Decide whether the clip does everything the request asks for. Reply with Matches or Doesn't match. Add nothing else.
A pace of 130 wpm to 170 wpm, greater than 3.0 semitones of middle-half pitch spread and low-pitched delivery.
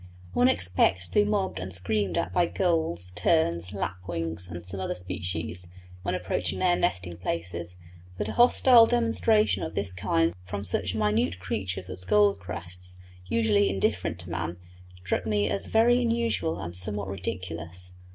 Matches